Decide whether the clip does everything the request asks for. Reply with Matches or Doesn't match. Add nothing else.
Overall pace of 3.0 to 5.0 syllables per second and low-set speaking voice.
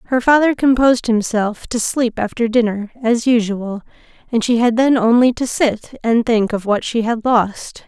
Doesn't match